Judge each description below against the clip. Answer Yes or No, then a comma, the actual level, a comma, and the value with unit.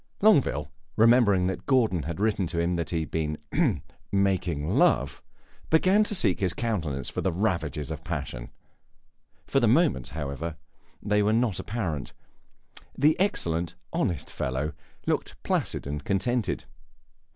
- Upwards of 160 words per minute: No, average, 140 wpm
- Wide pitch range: Yes, wide, 6.3 semitones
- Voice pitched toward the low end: Yes, very low, 90 Hz